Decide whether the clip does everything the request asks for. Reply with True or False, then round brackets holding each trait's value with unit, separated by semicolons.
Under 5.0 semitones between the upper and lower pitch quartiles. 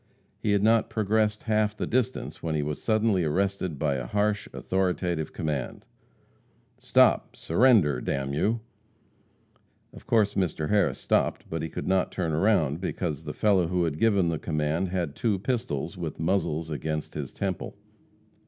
False (5.3 semitones)